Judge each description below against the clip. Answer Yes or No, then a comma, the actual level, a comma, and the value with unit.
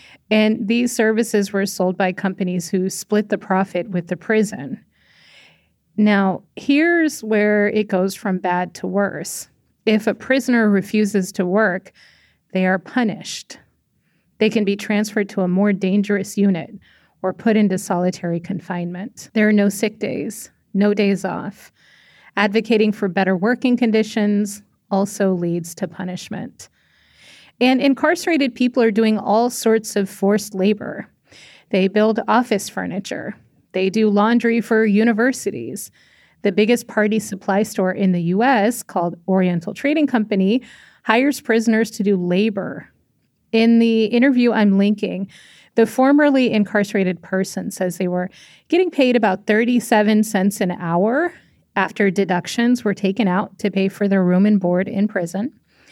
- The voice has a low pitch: No, high, 205 Hz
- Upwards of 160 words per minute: No, average, 140 wpm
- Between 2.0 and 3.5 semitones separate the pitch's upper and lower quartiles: Yes, average, 2.8 semitones